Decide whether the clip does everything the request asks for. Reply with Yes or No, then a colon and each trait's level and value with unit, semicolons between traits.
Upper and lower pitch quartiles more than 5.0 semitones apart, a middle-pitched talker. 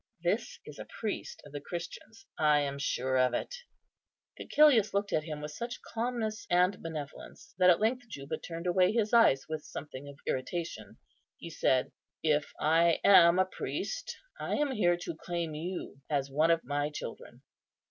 Yes: wide, 5.5 semitones; medium, 170 Hz